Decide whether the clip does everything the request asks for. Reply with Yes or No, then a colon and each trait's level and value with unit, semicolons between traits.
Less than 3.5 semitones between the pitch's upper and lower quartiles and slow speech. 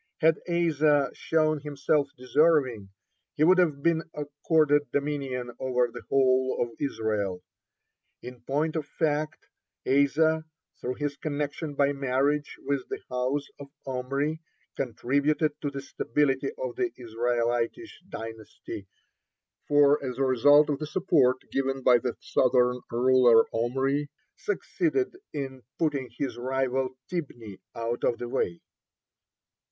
Yes: average, 2.9 semitones; slow, 125 wpm